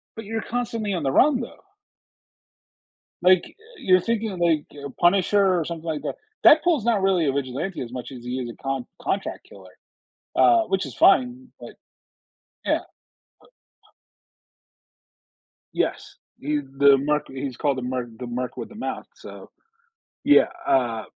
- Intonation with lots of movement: Yes, wide, 8.6 semitones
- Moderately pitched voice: Yes, medium, 170 Hz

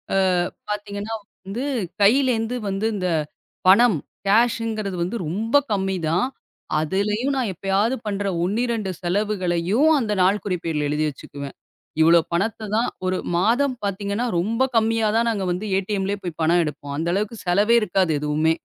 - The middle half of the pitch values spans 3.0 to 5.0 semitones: Yes, average, 4.0 semitones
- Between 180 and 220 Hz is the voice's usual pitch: Yes, high, 200 Hz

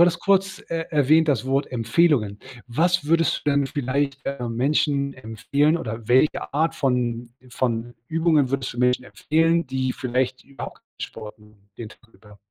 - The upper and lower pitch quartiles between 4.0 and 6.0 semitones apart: Yes, average, 4.3 semitones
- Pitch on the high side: No, low, 135 Hz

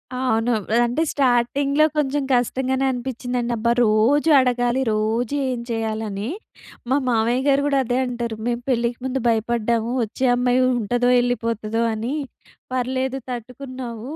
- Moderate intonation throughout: No, narrow, 2.2 semitones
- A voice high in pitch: Yes, high, 245 Hz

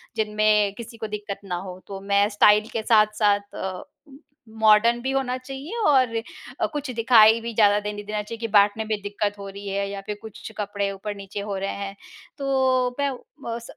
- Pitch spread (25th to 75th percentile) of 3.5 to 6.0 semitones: No, narrow, 2.5 semitones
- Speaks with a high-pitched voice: Yes, high, 210 Hz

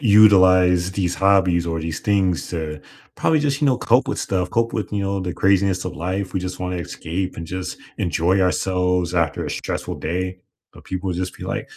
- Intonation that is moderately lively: No, narrow, 1.8 semitones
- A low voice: Yes, very low, 90 Hz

